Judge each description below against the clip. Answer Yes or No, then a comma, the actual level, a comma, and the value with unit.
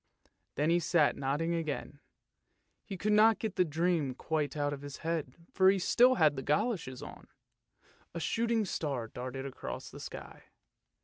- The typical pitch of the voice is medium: Yes, medium, 160 Hz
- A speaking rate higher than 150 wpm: Yes, average, 165 wpm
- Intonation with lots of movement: No, average, 4.9 semitones